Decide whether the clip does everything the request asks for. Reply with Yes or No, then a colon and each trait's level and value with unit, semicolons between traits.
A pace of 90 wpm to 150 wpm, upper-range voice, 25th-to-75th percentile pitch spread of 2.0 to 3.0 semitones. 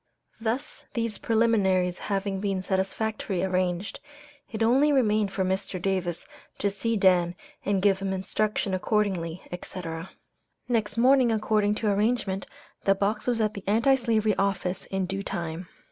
Yes: average, 145 wpm; high, 200 Hz; average, 2.7 semitones